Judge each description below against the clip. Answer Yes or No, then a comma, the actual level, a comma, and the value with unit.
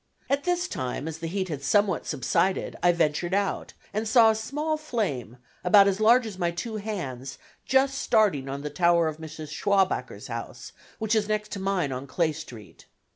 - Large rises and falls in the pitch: Yes, wide, 6.2 semitones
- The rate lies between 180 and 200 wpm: Yes, average, 185 wpm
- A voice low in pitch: No, high, 190 Hz